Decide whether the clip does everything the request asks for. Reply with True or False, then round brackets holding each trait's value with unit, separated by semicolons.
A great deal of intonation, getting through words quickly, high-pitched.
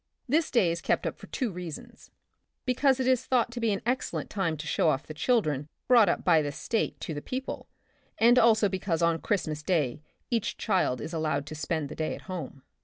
False (7.2 semitones; 225 wpm; 180 Hz)